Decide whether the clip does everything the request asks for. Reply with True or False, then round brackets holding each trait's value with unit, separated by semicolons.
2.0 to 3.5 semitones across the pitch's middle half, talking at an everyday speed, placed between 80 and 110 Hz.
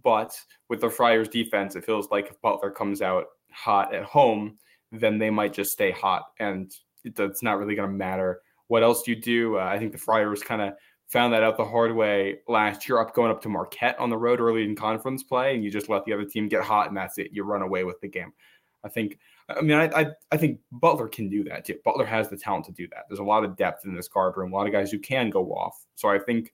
False (2.7 semitones; 265 wpm; 105 Hz)